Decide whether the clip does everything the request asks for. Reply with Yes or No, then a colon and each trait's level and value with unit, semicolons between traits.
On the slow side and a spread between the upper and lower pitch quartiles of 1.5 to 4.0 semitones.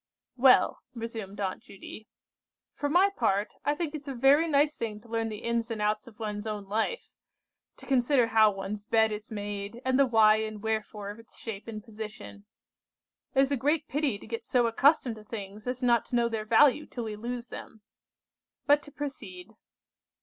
No: average, 195 wpm; average, 3.6 semitones